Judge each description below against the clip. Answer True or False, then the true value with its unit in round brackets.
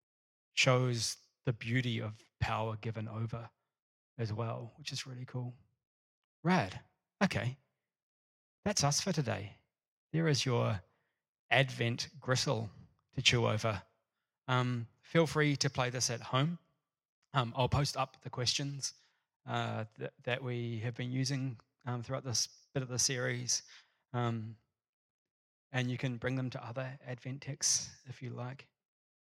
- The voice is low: True (125 Hz)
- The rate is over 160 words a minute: False (140 wpm)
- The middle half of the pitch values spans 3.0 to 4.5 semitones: False (2.6 semitones)